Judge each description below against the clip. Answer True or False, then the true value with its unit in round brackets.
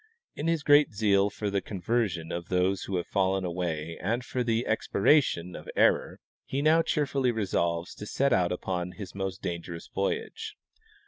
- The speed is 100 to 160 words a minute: False (170 wpm)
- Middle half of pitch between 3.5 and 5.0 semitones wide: False (5.5 semitones)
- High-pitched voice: False (100 Hz)